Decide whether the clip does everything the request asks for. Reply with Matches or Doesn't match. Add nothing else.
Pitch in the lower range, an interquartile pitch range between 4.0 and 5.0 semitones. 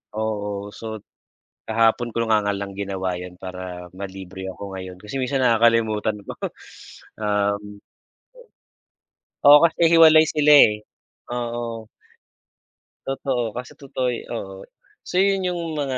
Matches